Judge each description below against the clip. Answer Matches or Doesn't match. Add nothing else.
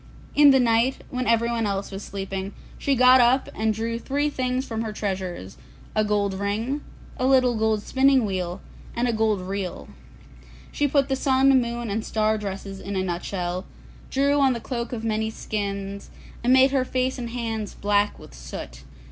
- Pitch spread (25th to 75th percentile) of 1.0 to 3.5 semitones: Doesn't match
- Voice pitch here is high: Matches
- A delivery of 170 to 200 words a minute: Matches